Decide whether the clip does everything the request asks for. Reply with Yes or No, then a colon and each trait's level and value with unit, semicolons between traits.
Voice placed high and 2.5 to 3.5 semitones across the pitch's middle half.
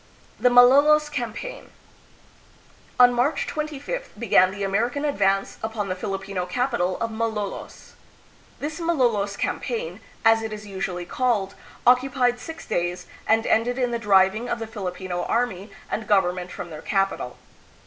No: high, 225 Hz; average, 4.4 semitones